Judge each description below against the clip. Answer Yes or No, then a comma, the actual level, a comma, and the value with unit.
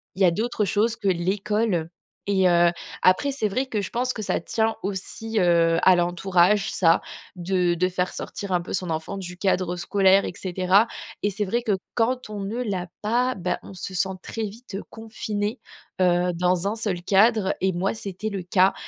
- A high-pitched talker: Yes, high, 195 Hz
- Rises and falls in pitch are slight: No, average, 3.2 semitones